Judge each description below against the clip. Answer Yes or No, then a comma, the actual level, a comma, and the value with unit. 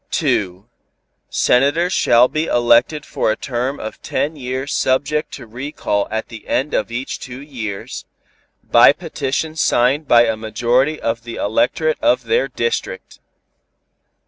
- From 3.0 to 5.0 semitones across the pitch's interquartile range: Yes, average, 4.4 semitones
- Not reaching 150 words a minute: Yes, average, 140 wpm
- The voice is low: Yes, low, 130 Hz